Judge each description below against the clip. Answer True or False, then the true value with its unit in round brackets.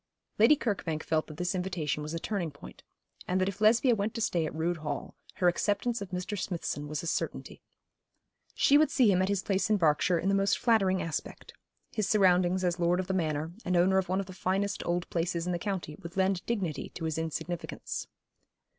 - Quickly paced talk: True (215 wpm)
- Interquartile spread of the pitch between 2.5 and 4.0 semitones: True (3.1 semitones)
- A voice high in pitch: False (180 Hz)